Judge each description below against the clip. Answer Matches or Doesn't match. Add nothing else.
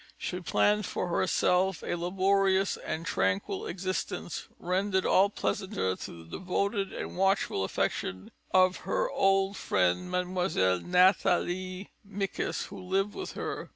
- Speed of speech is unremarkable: Doesn't match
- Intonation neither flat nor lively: Doesn't match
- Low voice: Doesn't match